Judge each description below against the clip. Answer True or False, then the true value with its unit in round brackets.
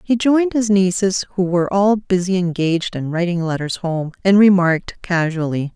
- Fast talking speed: False (165 wpm)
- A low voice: False (185 Hz)